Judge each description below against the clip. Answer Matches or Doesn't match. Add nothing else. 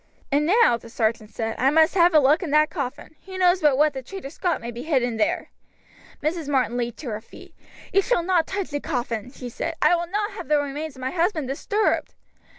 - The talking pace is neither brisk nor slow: Doesn't match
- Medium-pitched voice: Doesn't match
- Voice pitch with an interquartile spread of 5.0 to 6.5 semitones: Matches